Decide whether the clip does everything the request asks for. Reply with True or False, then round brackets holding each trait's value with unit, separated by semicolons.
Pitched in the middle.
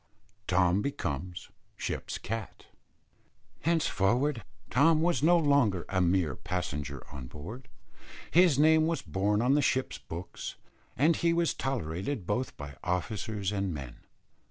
False (105 Hz)